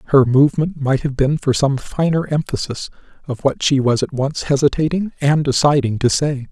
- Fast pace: No, average, 185 wpm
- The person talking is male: Yes, male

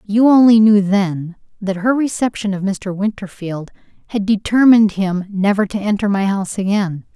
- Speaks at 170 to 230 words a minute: No, average, 160 wpm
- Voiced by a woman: Yes, female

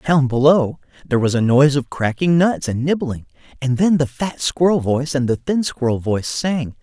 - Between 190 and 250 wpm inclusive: Yes, average, 200 wpm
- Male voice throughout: Yes, male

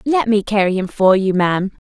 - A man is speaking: No, female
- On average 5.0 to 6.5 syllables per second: No, 4.7 syllables/s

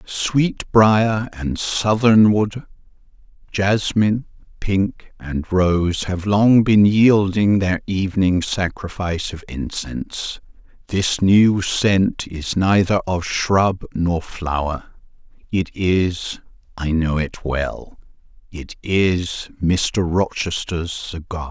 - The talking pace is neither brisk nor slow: No, slow, 100 wpm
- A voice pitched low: Yes, very low, 95 Hz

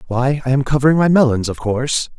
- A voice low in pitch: Yes, low, 130 Hz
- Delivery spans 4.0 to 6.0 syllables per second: No, 6.3 syllables/s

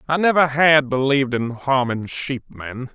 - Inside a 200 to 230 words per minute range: No, average, 165 wpm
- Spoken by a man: Yes, male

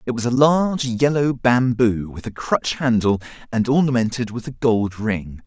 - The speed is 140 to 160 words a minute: No, average, 175 wpm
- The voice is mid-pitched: No, low, 120 Hz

